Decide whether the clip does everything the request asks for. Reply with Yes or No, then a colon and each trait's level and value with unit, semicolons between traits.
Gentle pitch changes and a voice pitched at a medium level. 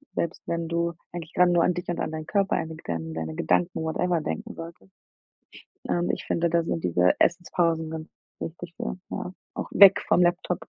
Yes: narrow, 1.7 semitones; medium, 170 Hz